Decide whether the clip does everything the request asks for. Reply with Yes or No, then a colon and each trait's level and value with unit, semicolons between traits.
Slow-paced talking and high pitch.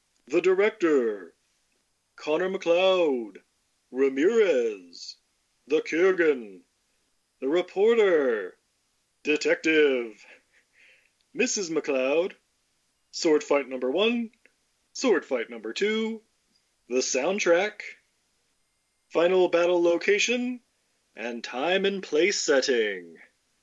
Yes: slow, 75 wpm; high, 200 Hz